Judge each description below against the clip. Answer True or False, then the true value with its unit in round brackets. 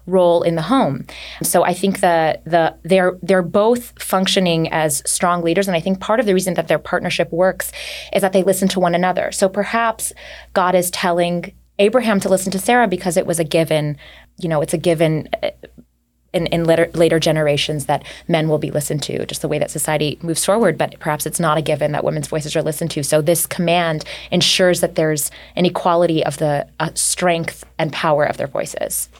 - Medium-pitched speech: True (170 Hz)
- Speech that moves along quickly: True (210 wpm)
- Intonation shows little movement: False (3.0 semitones)